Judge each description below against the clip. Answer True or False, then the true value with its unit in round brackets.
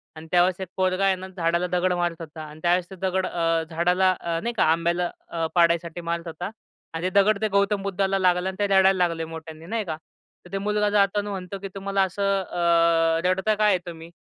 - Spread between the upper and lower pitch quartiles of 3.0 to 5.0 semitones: False (2.5 semitones)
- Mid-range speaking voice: True (180 Hz)